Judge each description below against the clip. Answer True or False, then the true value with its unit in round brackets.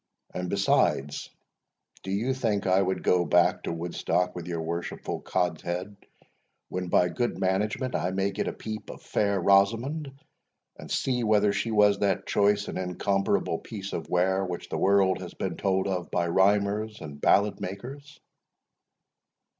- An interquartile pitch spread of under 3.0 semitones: True (2.5 semitones)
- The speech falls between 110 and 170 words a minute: True (160 wpm)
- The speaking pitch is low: True (95 Hz)